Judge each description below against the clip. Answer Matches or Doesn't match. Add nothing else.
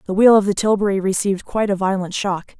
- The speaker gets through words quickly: Matches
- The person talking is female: Matches